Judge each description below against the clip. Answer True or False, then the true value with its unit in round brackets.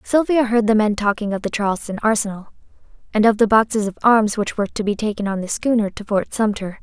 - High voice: True (215 Hz)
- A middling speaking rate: False (230 wpm)